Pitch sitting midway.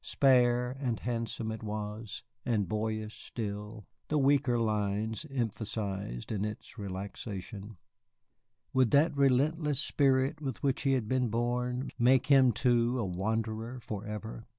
No: low, 115 Hz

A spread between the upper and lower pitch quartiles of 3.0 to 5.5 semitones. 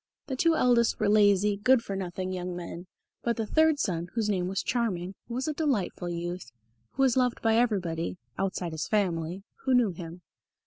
Yes: average, 5.2 semitones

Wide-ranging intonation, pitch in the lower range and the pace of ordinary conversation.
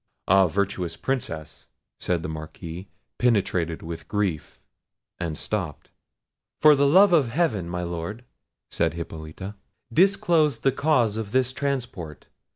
No: wide, 8.0 semitones; low, 100 Hz; slow, 125 wpm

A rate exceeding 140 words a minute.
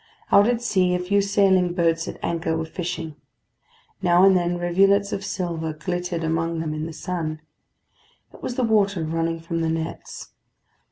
Yes: average, 170 wpm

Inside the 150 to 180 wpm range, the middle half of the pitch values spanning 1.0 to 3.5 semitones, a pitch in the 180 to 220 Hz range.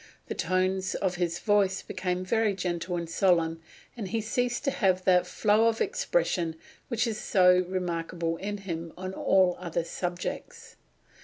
Yes: average, 155 wpm; average, 2.8 semitones; medium, 185 Hz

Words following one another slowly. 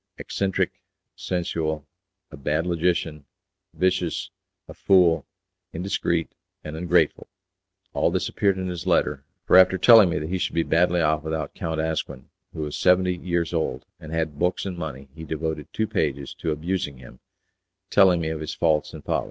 No: average, 170 wpm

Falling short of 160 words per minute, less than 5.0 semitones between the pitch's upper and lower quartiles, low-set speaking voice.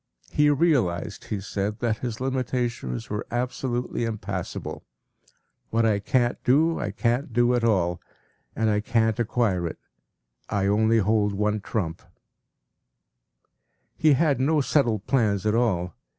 Yes: slow, 135 wpm; average, 3.3 semitones; low, 115 Hz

